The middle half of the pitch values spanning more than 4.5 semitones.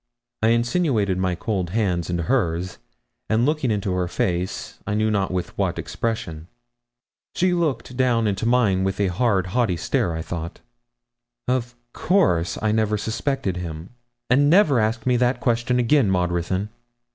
Yes: average, 5.3 semitones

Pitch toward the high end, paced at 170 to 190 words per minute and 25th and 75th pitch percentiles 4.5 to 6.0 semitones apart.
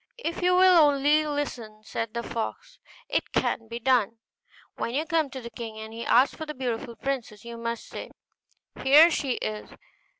Yes: very high, 255 Hz; average, 180 wpm; average, 4.8 semitones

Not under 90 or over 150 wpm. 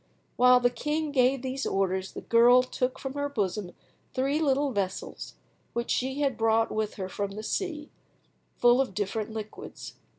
No: average, 165 wpm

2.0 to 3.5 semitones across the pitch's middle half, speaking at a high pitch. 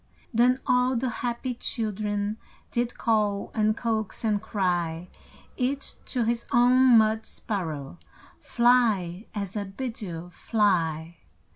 No: average, 4.0 semitones; high, 215 Hz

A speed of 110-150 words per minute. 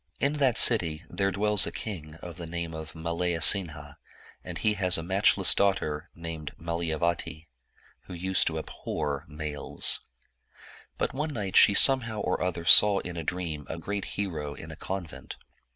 No: average, 160 wpm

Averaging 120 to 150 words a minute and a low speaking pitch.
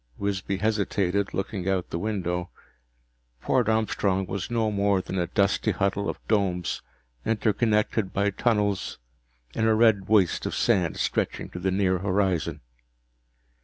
Yes: slow, 135 wpm; low, 100 Hz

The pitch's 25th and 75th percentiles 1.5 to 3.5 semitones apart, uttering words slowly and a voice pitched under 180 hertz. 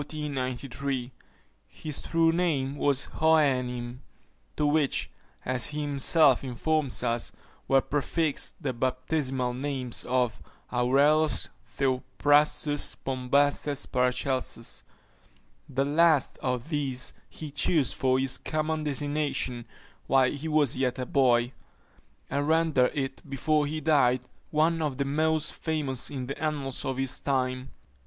Yes: average, 2.9 semitones; slow, 120 wpm; medium, 140 Hz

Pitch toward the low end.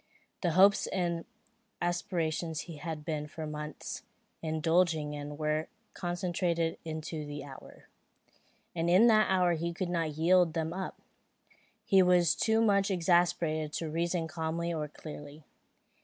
No: medium, 165 Hz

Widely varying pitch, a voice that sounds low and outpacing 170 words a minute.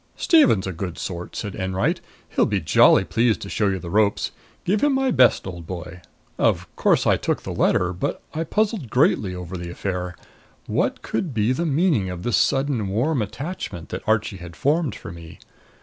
Yes: wide, 7.8 semitones; low, 105 Hz; average, 190 wpm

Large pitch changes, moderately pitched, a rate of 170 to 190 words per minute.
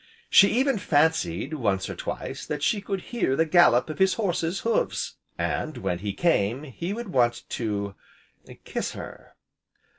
No: wide, 8.3 semitones; medium, 155 Hz; average, 155 wpm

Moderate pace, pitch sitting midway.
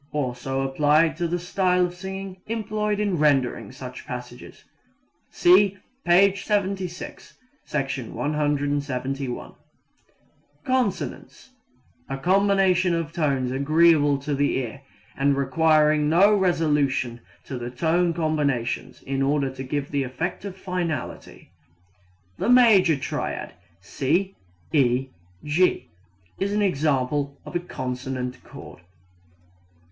No: slow, 110 wpm; medium, 150 Hz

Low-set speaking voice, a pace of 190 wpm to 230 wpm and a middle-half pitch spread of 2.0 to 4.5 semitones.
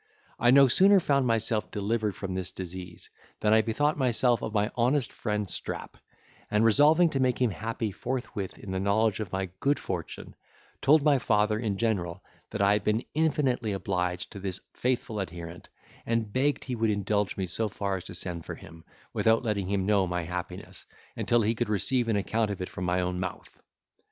Yes: low, 105 Hz; average, 195 wpm; average, 4.2 semitones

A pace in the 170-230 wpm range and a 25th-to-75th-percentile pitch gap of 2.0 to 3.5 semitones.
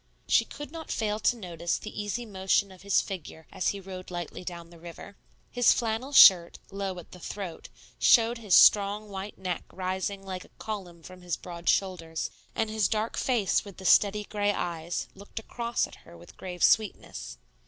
Yes: average, 185 wpm; average, 3.1 semitones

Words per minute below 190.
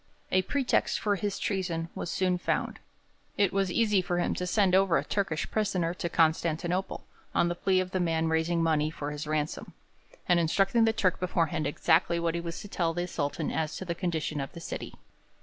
No: average, 200 wpm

